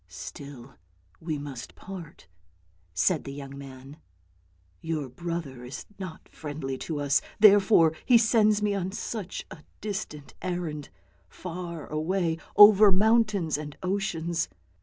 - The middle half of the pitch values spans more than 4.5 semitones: Yes, wide, 5.5 semitones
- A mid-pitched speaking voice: Yes, medium, 165 Hz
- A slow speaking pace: Yes, slow, 130 wpm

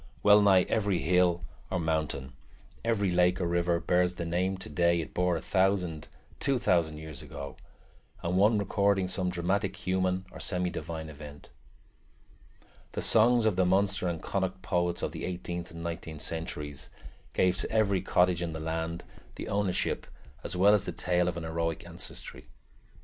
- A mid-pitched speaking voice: No, very low, 90 Hz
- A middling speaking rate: Yes, average, 165 wpm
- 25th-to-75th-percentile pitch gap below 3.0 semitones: Yes, narrow, 2.4 semitones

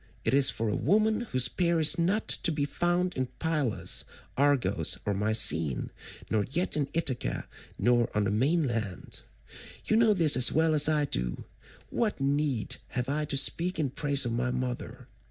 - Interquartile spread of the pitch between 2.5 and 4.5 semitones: No, average, 5.3 semitones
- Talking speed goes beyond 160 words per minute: Yes, average, 170 wpm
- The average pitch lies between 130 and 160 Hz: Yes, medium, 140 Hz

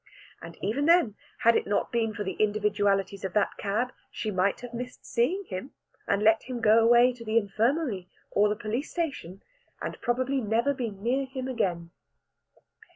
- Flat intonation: No, average, 3.8 semitones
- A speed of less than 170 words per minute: No, average, 175 wpm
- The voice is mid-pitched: No, high, 225 Hz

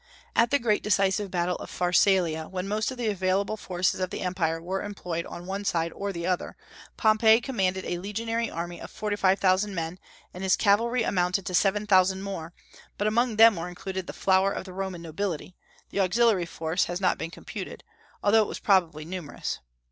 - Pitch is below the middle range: No, high, 190 Hz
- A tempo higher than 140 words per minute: Yes, average, 195 wpm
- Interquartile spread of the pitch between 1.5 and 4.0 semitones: Yes, average, 2.7 semitones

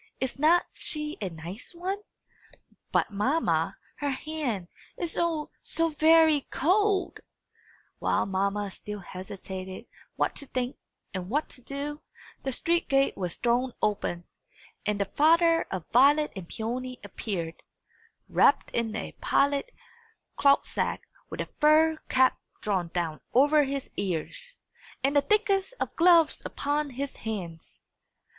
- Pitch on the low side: No, very high, 275 Hz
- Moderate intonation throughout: No, wide, 7.6 semitones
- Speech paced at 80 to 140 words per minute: Yes, slow, 135 wpm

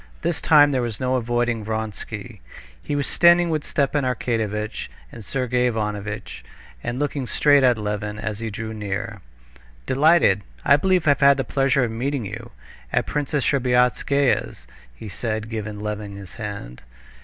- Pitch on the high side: No, low, 120 Hz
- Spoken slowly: No, average, 155 wpm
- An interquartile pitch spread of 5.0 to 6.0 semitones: No, average, 4.6 semitones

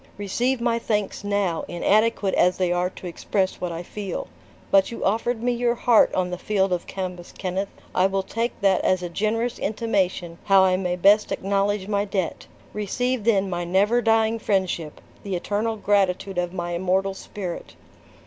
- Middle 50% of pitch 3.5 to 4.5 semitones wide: No, average, 2.8 semitones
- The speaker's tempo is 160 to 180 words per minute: Yes, average, 175 wpm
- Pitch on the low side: No, high, 195 Hz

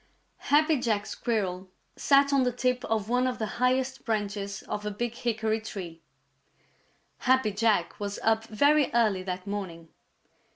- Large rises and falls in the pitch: No, average, 3.8 semitones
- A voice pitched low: No, high, 220 Hz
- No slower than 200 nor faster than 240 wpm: No, average, 155 wpm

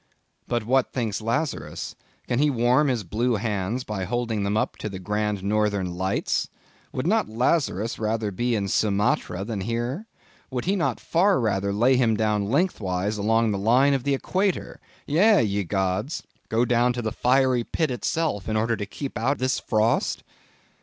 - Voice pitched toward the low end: Yes, low, 115 Hz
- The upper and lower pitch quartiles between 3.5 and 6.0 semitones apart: Yes, average, 4.0 semitones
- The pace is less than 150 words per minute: No, average, 175 wpm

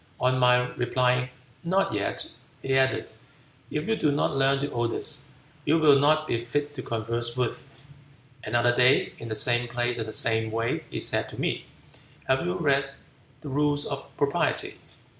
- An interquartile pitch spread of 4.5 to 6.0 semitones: No, average, 3.3 semitones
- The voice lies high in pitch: No, low, 130 Hz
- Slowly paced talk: No, average, 170 wpm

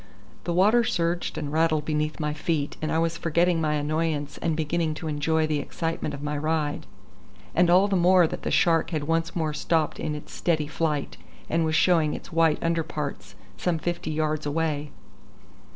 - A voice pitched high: No, medium, 160 Hz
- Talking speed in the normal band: Yes, average, 185 wpm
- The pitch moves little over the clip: Yes, narrow, 1.8 semitones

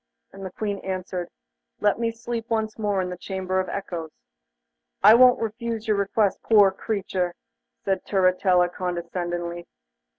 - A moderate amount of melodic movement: Yes, average, 3.2 semitones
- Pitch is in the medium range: No, high, 195 Hz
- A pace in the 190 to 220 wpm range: No, average, 140 wpm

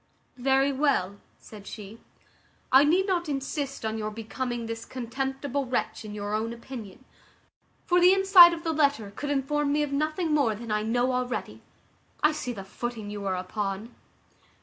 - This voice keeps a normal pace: Yes, average, 170 wpm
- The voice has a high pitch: Yes, very high, 255 Hz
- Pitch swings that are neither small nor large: Yes, average, 5.0 semitones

